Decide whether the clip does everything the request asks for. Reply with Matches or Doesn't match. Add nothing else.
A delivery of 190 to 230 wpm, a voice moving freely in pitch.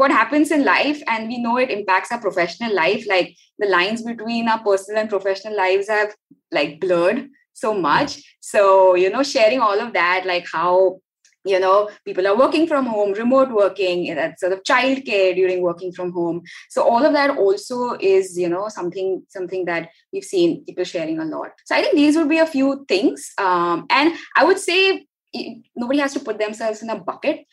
Matches